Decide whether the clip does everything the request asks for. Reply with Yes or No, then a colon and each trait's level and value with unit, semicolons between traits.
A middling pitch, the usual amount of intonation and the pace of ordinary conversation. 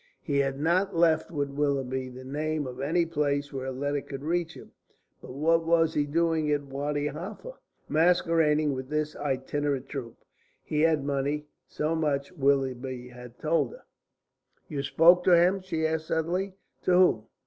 Yes: medium, 150 Hz; average, 3.0 semitones; average, 165 wpm